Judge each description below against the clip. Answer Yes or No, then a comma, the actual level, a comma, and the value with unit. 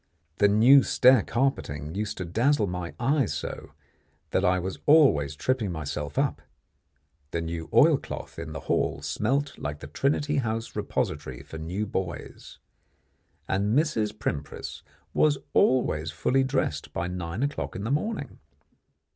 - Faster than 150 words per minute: No, average, 145 wpm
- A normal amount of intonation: No, wide, 8.1 semitones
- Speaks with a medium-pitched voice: No, low, 105 Hz